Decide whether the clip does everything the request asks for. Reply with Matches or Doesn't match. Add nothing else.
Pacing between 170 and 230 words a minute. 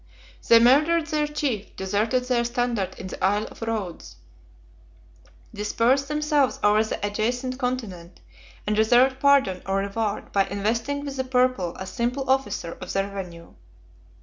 Doesn't match